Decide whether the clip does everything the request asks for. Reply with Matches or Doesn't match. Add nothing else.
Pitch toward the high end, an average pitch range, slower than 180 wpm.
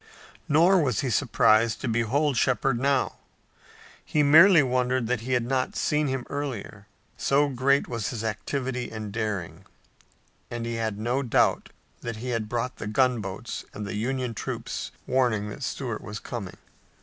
Doesn't match